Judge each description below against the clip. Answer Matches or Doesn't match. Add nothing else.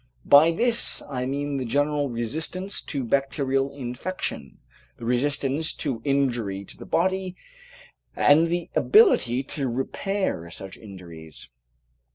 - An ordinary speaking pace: Doesn't match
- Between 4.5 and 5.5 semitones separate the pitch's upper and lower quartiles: Matches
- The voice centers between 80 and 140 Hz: Matches